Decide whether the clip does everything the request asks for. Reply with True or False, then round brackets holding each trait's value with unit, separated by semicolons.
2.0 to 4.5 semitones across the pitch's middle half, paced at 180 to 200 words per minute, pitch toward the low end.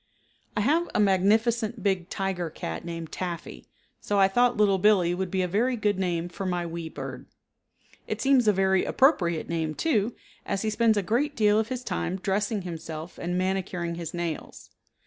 False (3.9 semitones; 185 wpm; 190 Hz)